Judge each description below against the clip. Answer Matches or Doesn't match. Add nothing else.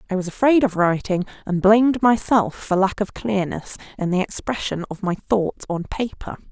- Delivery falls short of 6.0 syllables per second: Matches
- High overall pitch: Matches